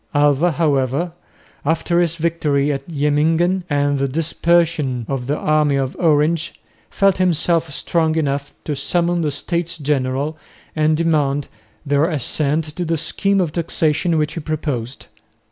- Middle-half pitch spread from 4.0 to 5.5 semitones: No, average, 2.9 semitones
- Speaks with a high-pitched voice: No, medium, 155 Hz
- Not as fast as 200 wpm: Yes, average, 140 wpm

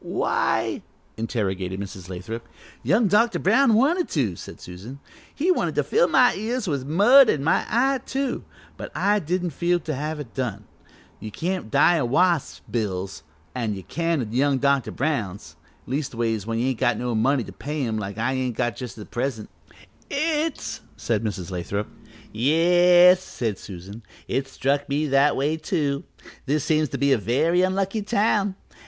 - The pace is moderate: Yes, average, 175 wpm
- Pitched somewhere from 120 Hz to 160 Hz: Yes, medium, 140 Hz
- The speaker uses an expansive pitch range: Yes, wide, 8.1 semitones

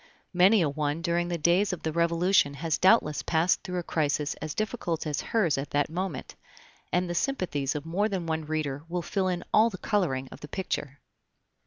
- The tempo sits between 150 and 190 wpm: No, average, 200 wpm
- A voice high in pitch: No, medium, 170 Hz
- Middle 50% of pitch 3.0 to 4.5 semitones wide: Yes, average, 3.7 semitones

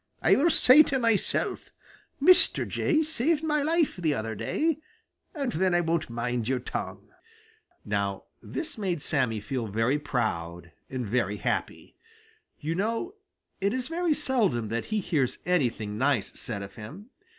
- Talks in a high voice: No, medium, 160 Hz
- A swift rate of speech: No, average, 150 wpm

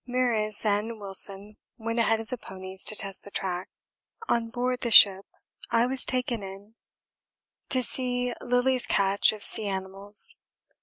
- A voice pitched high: Yes, high, 215 Hz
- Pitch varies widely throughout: No, average, 3.8 semitones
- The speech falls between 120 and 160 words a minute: Yes, average, 150 wpm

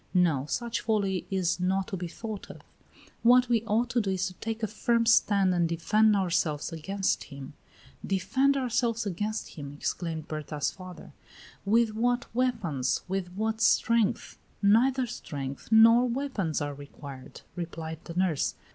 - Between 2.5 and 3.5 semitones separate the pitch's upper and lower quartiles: No, wide, 5.4 semitones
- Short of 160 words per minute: Yes, average, 150 wpm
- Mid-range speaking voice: No, high, 195 Hz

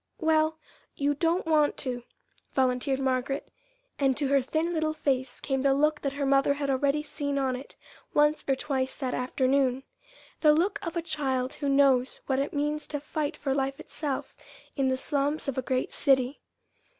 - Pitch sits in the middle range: No, very high, 280 Hz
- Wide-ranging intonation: No, narrow, 2.2 semitones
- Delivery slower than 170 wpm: No, average, 180 wpm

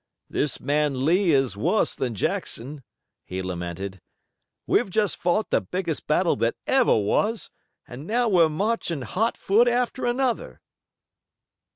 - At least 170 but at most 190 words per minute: No, slow, 135 wpm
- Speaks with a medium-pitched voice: Yes, medium, 165 Hz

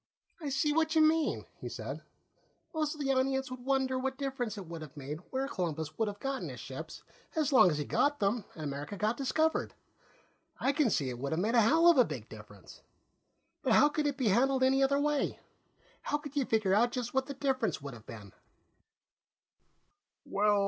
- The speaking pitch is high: Yes, very high, 260 Hz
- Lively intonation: Yes, wide, 7.7 semitones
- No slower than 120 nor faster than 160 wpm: No, fast, 205 wpm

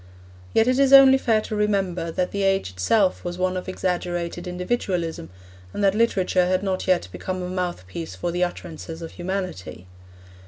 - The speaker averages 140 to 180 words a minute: Yes, average, 170 wpm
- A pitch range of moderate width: No, narrow, 2.2 semitones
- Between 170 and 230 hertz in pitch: Yes, medium, 185 Hz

